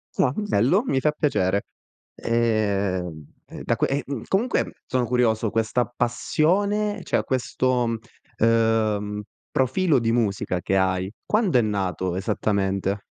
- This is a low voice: Yes, low, 115 Hz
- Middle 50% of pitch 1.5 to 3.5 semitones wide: No, average, 4.4 semitones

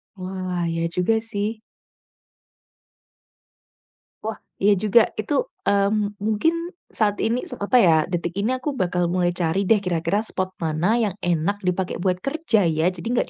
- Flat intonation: No, average, 3.5 semitones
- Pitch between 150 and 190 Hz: No, high, 200 Hz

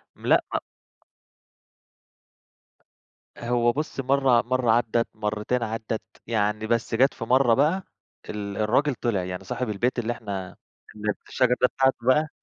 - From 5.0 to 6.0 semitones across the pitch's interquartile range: No, average, 3.1 semitones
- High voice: No, low, 115 Hz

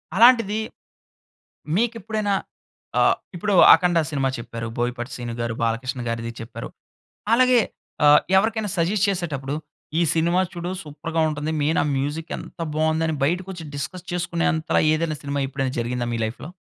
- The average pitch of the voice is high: No, medium, 160 Hz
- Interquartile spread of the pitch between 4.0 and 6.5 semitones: Yes, wide, 5.6 semitones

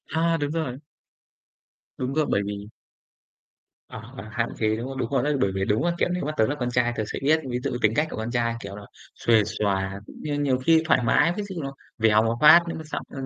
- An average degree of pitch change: No, wide, 5.8 semitones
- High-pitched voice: No, low, 125 Hz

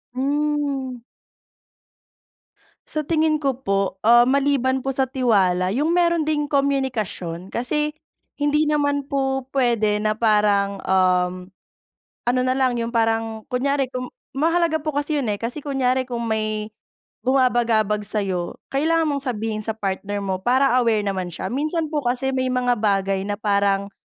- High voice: Yes, very high, 250 Hz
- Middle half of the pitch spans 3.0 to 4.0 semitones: No, average, 5.0 semitones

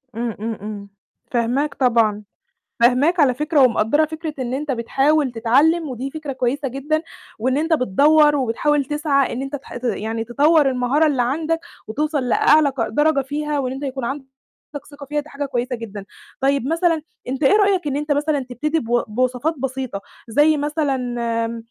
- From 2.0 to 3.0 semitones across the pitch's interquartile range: No, average, 3.7 semitones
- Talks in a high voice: Yes, very high, 275 Hz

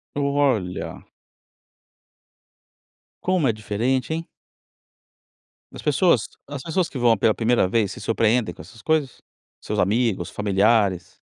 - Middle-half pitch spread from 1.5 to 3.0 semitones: No, wide, 5.4 semitones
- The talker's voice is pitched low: Yes, low, 115 Hz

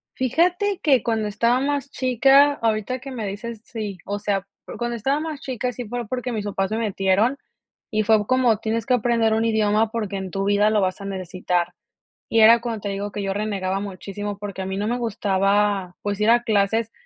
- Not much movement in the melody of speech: No, average, 3.1 semitones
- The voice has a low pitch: No, high, 215 Hz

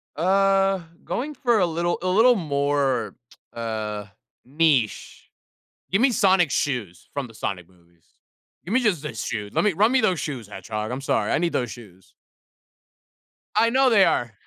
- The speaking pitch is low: No, medium, 145 Hz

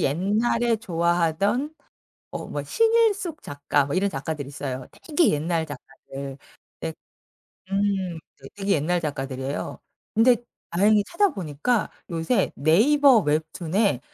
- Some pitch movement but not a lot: No, wide, 7.7 semitones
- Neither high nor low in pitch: Yes, medium, 175 Hz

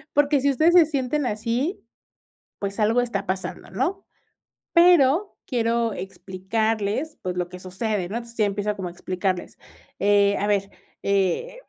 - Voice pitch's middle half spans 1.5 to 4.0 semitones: No, wide, 5.6 semitones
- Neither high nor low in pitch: No, high, 220 Hz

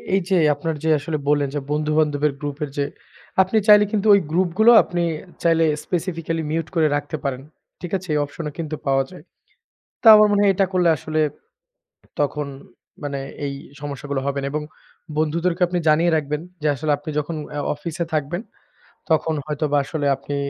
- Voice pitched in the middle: Yes, medium, 155 Hz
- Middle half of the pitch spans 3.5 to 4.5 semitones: No, average, 3.0 semitones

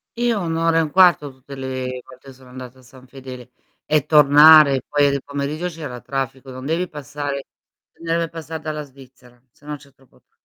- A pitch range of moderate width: Yes, average, 3.1 semitones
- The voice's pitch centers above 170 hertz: No, medium, 140 Hz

